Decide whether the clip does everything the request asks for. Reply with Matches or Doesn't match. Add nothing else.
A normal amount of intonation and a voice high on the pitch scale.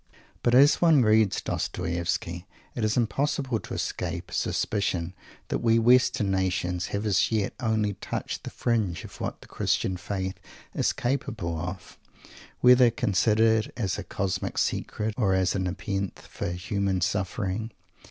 Doesn't match